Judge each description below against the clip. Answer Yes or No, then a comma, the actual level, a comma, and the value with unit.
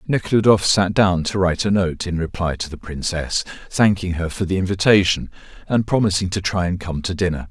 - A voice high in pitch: No, very low, 90 Hz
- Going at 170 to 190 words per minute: No, average, 200 wpm